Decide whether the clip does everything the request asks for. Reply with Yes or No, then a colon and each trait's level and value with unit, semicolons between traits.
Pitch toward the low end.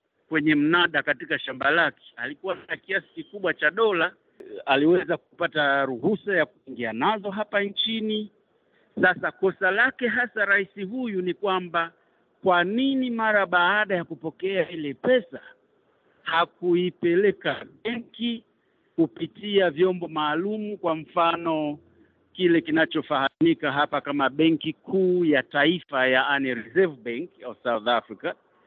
No: medium, 180 Hz